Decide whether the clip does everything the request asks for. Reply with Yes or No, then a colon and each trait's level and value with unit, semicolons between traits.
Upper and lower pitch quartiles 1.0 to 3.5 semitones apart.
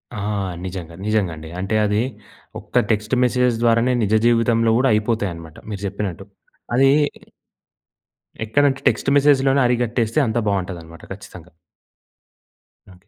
No: average, 4.3 semitones